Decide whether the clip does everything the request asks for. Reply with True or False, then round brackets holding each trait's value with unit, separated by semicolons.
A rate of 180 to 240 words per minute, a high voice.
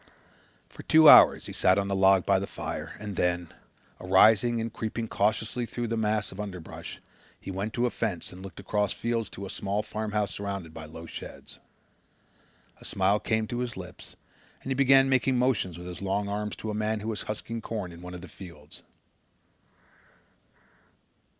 False (185 wpm; 105 Hz)